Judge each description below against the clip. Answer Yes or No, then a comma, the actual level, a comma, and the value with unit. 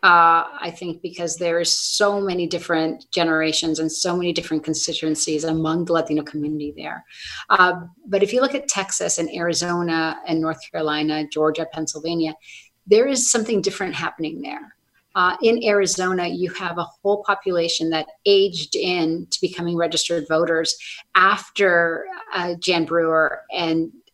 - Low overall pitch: No, medium, 170 Hz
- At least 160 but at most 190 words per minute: No, average, 150 wpm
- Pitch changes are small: Yes, narrow, 2.2 semitones